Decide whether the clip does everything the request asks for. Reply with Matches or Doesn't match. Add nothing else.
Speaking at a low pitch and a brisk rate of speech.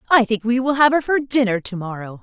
Doesn't match